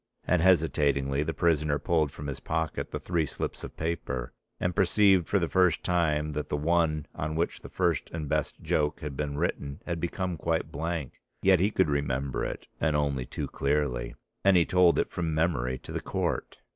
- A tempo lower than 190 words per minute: No, average, 195 wpm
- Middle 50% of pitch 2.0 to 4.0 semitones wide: Yes, average, 3.1 semitones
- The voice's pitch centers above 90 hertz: No, very low, 80 Hz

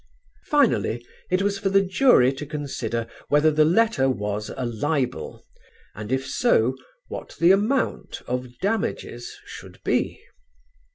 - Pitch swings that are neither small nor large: No, wide, 8.0 semitones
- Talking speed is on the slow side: Yes, slow, 130 wpm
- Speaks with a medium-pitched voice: Yes, medium, 145 Hz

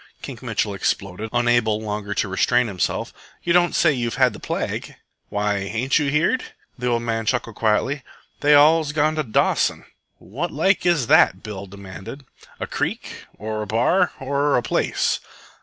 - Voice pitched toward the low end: Yes, low, 120 Hz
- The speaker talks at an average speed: Yes, average, 165 wpm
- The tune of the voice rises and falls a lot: Yes, wide, 5.7 semitones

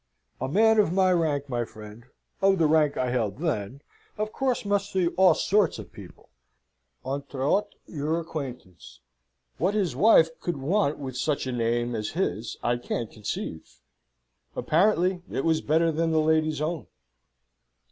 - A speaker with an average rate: Yes, average, 155 wpm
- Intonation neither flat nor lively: No, wide, 6.2 semitones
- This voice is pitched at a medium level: Yes, medium, 155 Hz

